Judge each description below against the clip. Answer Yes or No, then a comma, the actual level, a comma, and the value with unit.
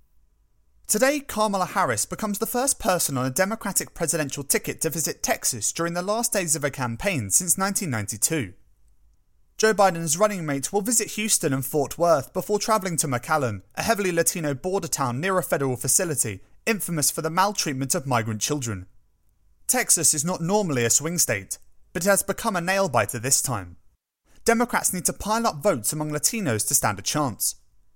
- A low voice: No, medium, 165 Hz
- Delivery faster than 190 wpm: No, average, 175 wpm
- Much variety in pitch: Yes, wide, 7.7 semitones